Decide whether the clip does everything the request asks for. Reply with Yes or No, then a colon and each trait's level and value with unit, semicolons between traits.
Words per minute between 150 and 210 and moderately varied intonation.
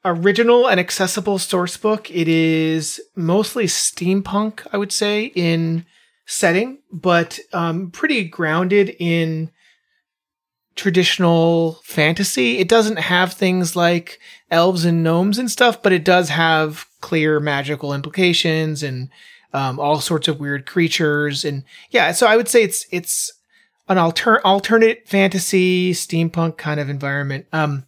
No: slow, 135 wpm; average, 4.2 semitones